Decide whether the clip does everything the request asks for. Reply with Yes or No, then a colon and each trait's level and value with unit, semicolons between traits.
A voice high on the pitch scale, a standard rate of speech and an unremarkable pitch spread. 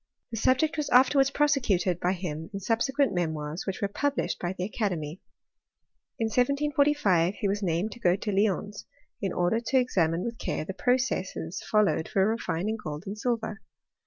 No: high, 205 Hz; average, 165 wpm; wide, 5.8 semitones